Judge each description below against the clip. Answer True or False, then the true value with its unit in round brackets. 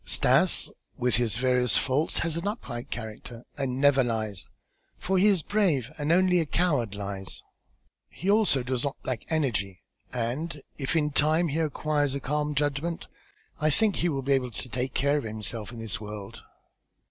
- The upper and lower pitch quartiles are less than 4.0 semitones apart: False (4.8 semitones)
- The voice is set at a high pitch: False (135 Hz)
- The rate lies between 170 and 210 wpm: True (175 wpm)